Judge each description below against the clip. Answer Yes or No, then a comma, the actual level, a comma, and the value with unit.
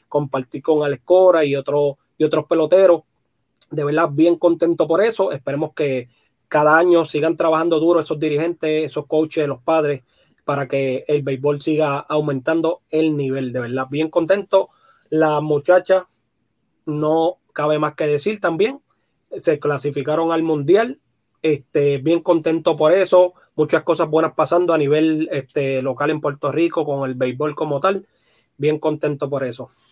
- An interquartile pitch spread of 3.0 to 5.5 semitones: No, narrow, 2.6 semitones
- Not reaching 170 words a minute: Yes, average, 155 wpm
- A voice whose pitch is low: No, medium, 155 Hz